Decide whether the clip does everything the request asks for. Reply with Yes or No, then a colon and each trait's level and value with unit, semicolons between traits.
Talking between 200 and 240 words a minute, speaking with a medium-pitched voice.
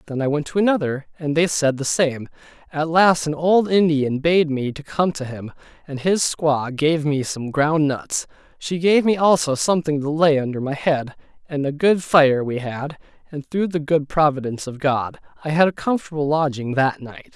Yes: fast, 205 wpm; medium, 150 Hz